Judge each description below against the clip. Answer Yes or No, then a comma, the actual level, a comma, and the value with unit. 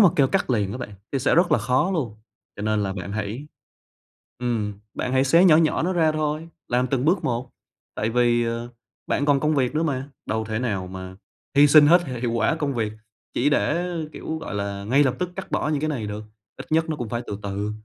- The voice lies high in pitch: No, low, 125 Hz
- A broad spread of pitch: Yes, wide, 6.0 semitones